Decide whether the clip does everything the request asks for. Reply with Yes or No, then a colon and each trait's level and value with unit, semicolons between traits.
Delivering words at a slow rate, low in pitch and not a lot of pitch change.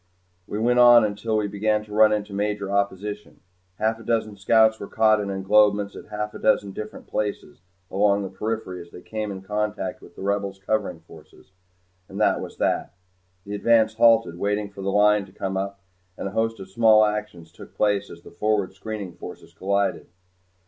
No: average, 190 wpm; low, 105 Hz; narrow, 1.6 semitones